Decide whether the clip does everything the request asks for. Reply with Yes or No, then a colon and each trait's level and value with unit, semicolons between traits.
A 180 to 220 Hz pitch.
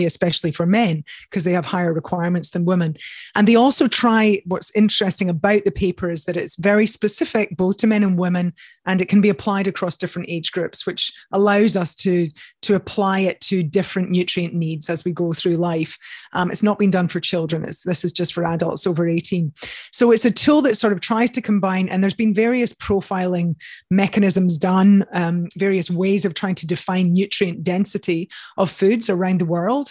Yes: medium, 185 Hz